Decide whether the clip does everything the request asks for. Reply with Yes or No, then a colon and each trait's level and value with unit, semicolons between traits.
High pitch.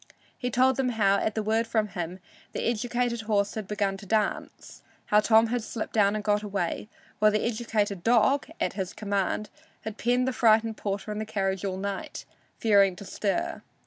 Yes: high, 215 Hz